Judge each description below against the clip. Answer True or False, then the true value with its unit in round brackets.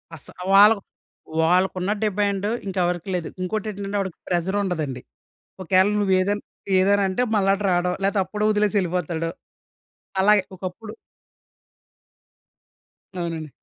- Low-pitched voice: False (190 Hz)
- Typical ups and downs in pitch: False (2.3 semitones)